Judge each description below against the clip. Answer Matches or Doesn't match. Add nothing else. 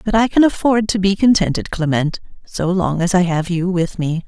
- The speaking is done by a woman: Matches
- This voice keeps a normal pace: Doesn't match